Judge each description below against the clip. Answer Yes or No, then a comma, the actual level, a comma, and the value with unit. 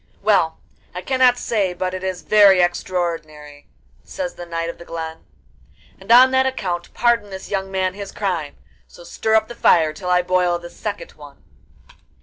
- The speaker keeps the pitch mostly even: No, average, 3.4 semitones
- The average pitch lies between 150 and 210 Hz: Yes, medium, 185 Hz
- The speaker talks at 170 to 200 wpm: Yes, average, 175 wpm